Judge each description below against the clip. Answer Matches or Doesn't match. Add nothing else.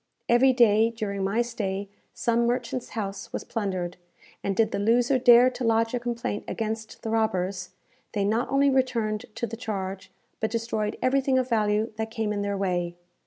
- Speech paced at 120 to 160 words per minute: Doesn't match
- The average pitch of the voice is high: Matches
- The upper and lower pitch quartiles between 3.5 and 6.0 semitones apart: Doesn't match